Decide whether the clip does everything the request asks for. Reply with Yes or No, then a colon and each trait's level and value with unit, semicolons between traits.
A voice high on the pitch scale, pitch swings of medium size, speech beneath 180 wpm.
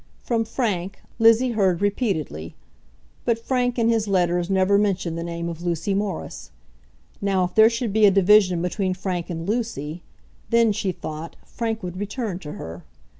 Yes: high, 195 Hz; average, 4.3 semitones; average, 165 wpm